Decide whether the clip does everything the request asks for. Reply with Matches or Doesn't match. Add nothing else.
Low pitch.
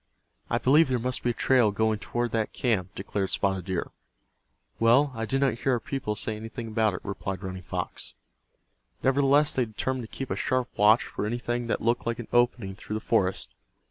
Matches